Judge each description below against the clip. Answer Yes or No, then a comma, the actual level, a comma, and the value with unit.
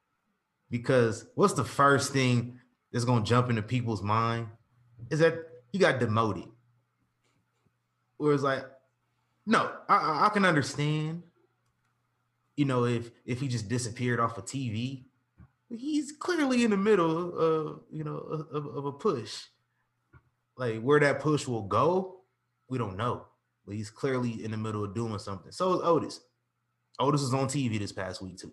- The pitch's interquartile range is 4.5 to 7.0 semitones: No, average, 3.9 semitones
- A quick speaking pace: No, average, 160 wpm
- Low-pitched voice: Yes, low, 125 Hz